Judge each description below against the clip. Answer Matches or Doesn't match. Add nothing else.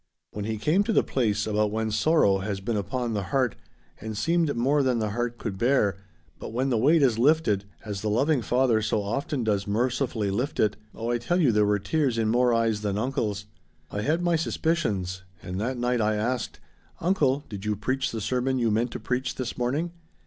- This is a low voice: Matches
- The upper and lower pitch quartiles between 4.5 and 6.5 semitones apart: Doesn't match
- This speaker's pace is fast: Matches